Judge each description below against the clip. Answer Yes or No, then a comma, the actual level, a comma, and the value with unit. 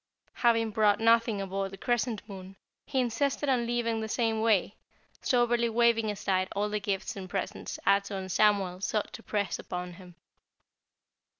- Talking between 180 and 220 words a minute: No, average, 165 wpm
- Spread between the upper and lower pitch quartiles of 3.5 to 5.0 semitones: No, average, 3.0 semitones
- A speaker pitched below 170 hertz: No, high, 210 Hz